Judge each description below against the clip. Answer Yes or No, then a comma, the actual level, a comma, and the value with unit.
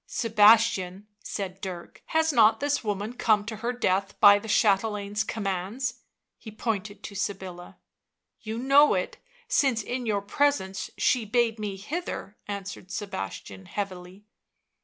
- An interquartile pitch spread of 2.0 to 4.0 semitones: Yes, average, 3.1 semitones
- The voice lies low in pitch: No, high, 210 Hz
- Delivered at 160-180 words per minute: No, average, 145 wpm